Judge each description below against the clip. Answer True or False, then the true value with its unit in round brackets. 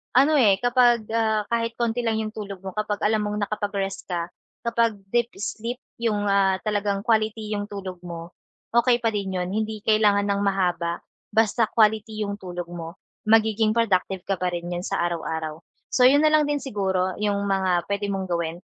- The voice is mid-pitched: False (205 Hz)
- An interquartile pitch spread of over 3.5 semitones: False (2.8 semitones)